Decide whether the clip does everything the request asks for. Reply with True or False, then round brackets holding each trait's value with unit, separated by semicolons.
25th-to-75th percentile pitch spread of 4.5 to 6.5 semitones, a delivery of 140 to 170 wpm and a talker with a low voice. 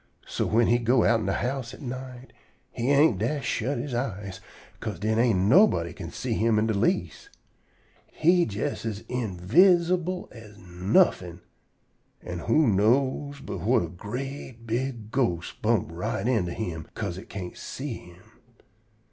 True (5.4 semitones; 155 wpm; 115 Hz)